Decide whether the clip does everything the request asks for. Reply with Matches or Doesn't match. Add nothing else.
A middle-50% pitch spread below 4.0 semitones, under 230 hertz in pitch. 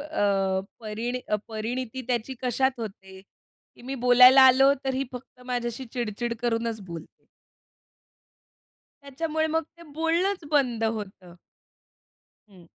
Doesn't match